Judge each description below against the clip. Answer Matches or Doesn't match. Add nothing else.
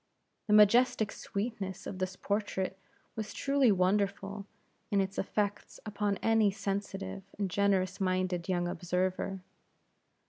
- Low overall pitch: Doesn't match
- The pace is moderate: Doesn't match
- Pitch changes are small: Matches